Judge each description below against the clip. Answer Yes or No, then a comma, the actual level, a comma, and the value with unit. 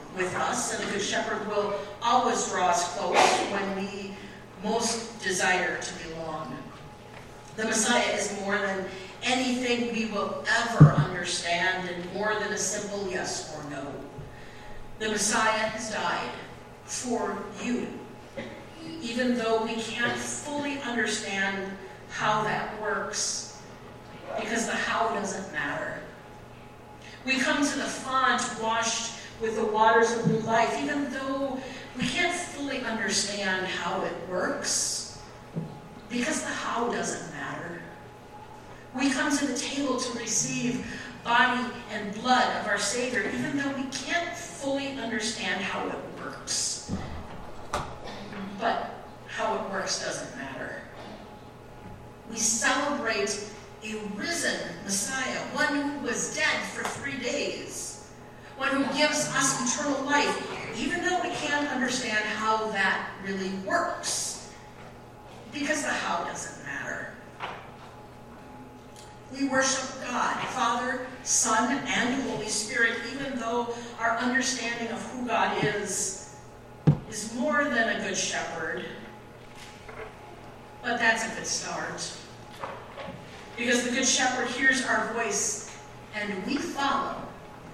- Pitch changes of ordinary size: Yes, average, 4.3 semitones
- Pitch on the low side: No, high, 230 Hz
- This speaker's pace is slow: Yes, slow, 120 wpm